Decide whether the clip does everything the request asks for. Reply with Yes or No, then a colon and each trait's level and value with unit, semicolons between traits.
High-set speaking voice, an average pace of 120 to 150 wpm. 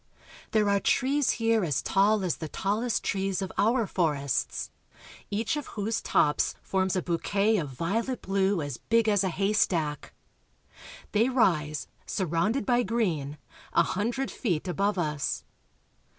Yes: high, 195 Hz; average, 145 wpm